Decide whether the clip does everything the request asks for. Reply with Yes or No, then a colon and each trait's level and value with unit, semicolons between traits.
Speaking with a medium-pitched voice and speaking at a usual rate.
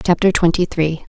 Yes: medium, 170 Hz; average, 155 wpm